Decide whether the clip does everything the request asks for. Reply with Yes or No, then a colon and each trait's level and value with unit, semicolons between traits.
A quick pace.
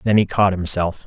Yes: fast, 225 wpm